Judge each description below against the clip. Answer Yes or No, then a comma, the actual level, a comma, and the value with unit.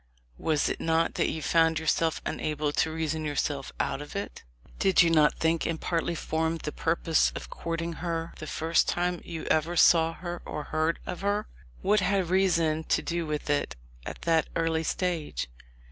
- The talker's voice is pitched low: No, medium, 165 Hz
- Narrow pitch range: Yes, narrow, 1.5 semitones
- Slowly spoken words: No, average, 185 wpm